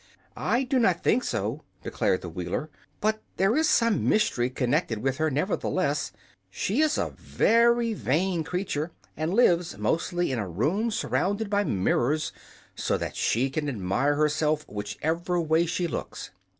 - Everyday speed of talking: Yes, average, 150 wpm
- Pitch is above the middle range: No, medium, 160 Hz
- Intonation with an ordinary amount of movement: No, wide, 7.2 semitones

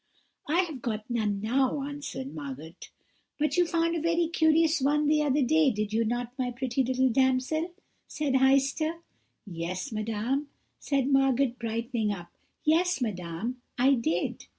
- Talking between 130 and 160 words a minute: Yes, average, 150 wpm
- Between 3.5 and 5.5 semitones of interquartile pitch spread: Yes, average, 4.9 semitones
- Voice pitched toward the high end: Yes, very high, 260 Hz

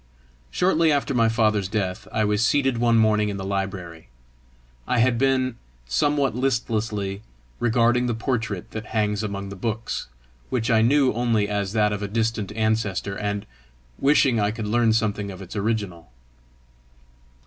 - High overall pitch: No, low, 110 Hz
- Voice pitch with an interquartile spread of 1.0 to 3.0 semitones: Yes, average, 2.7 semitones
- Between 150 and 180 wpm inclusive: Yes, average, 155 wpm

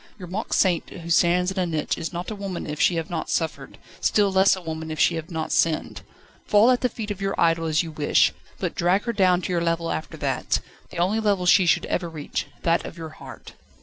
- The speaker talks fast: Yes, fast, 245 wpm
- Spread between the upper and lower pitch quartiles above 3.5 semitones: No, average, 2.9 semitones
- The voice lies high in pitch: No, medium, 175 Hz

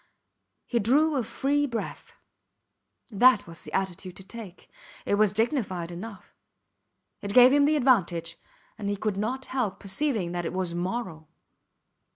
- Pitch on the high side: Yes, high, 210 Hz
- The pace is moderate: Yes, average, 150 wpm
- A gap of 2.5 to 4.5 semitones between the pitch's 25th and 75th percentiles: No, wide, 5.5 semitones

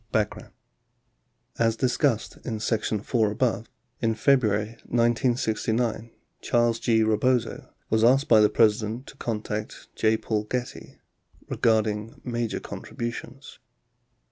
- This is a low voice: Yes, low, 115 Hz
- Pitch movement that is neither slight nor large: No, narrow, 1.7 semitones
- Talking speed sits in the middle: No, slow, 110 wpm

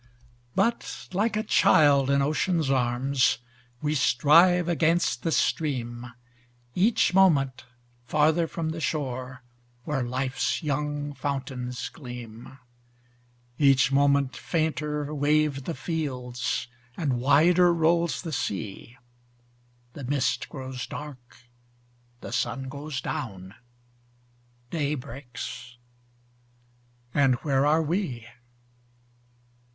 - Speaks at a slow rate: Yes, slow, 95 wpm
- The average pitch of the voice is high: No, medium, 140 Hz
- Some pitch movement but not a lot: Yes, average, 3.6 semitones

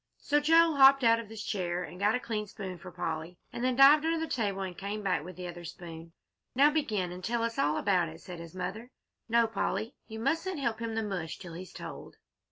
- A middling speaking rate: No, fast, 235 wpm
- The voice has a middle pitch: No, high, 210 Hz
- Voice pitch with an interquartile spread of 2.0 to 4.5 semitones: No, average, 5.2 semitones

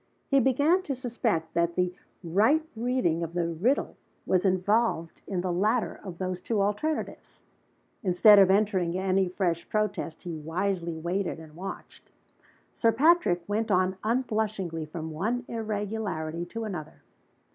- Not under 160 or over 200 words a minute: No, average, 140 wpm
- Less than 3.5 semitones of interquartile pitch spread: No, average, 4.5 semitones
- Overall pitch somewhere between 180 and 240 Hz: Yes, high, 190 Hz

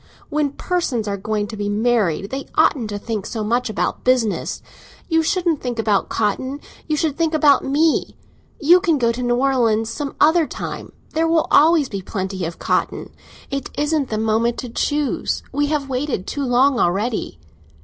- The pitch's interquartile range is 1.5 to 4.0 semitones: No, wide, 5.4 semitones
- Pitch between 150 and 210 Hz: No, very high, 255 Hz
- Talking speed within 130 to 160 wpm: No, average, 170 wpm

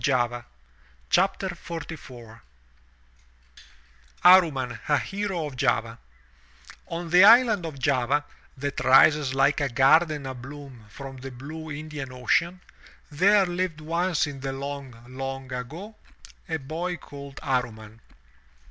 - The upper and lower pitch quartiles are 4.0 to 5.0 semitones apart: Yes, average, 4.6 semitones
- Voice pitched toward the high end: No, medium, 140 Hz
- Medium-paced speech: No, slow, 120 wpm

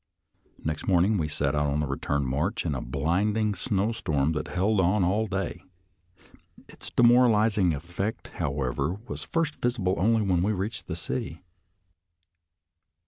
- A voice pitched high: No, very low, 90 Hz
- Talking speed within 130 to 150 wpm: Yes, average, 140 wpm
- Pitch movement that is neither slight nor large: No, wide, 5.9 semitones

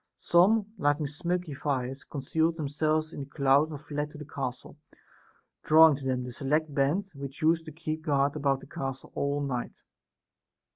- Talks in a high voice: No, medium, 145 Hz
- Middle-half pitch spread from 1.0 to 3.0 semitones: Yes, narrow, 2.4 semitones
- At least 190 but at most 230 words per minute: No, average, 165 wpm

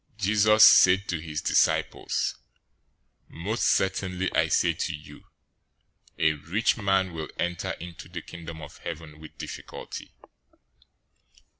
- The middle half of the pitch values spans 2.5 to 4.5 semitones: Yes, average, 3.3 semitones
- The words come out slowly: Yes, slow, 125 wpm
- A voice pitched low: Yes, very low, 90 Hz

